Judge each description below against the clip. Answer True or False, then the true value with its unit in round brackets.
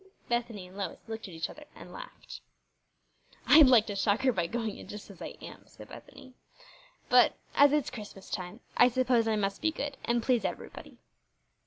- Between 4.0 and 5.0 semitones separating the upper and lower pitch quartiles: True (4.3 semitones)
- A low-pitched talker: False (230 Hz)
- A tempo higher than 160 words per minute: True (190 wpm)